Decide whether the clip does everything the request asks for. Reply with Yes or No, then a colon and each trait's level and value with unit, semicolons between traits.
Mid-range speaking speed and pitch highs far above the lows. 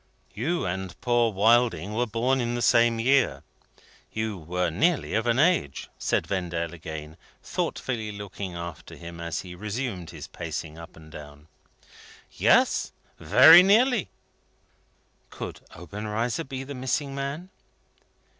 No: slow, 130 wpm; wide, 7.0 semitones